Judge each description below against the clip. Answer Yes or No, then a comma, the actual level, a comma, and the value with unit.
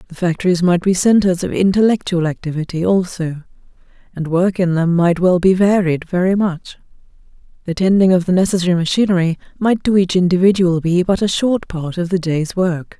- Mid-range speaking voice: Yes, medium, 180 Hz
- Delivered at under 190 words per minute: Yes, average, 175 wpm